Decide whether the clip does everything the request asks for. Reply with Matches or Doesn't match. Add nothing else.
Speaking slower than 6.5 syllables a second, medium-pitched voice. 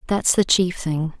Matches